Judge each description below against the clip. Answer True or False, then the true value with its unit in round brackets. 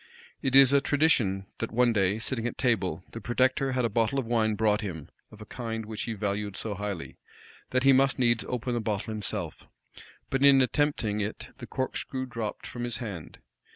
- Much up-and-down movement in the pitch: False (3.6 semitones)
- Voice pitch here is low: True (115 Hz)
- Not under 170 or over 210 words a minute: True (195 wpm)